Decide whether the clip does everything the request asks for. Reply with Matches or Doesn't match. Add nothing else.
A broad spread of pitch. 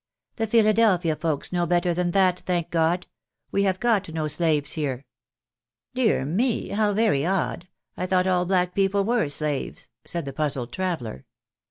Doesn't match